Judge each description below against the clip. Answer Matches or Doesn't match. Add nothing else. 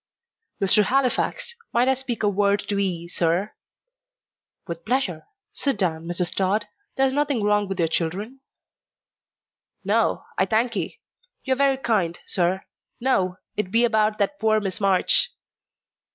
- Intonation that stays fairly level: Doesn't match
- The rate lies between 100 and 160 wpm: Matches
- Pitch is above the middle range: Matches